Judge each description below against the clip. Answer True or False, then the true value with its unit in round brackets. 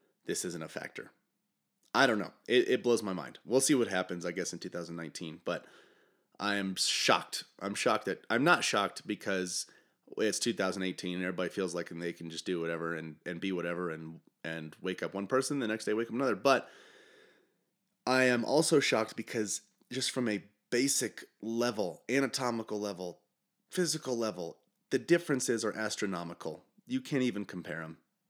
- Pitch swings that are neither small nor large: False (6.0 semitones)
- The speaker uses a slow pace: False (175 wpm)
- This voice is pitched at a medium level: False (105 Hz)